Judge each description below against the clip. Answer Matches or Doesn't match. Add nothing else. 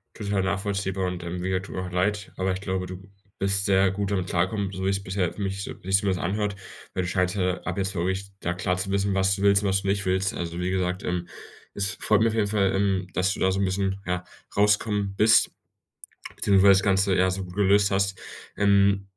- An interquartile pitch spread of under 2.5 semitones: Matches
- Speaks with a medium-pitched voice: Doesn't match